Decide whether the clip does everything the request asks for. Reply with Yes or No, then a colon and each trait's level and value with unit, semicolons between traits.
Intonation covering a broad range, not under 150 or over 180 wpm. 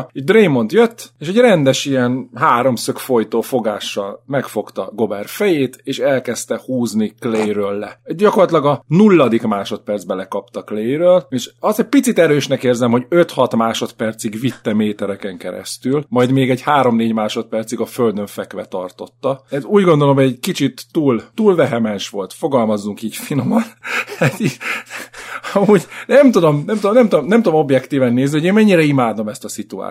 Yes: wide, 7.4 semitones; fast, 155 wpm